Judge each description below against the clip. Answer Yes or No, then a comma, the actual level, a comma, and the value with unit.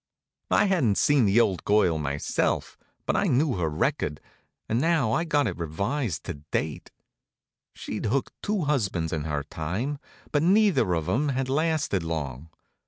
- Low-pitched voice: Yes, low, 110 Hz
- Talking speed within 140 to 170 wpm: Yes, average, 160 wpm